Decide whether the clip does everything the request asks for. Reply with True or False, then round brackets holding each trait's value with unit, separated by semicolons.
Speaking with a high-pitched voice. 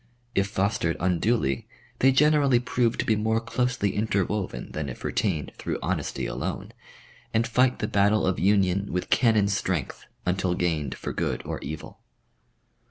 False (100 Hz)